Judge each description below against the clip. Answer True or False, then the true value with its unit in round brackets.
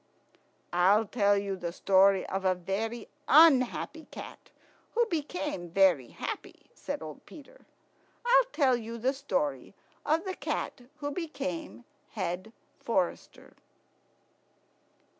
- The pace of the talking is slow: True (115 wpm)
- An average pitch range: False (7.9 semitones)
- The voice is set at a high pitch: True (225 Hz)